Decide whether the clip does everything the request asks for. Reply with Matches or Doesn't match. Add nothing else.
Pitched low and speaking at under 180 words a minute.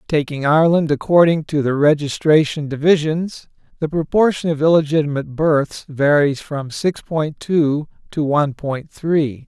Doesn't match